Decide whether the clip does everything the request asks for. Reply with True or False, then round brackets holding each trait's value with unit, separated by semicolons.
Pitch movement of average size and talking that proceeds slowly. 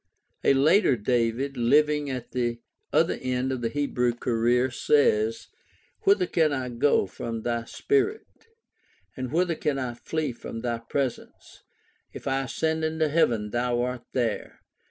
False (4.0 semitones; 145 wpm)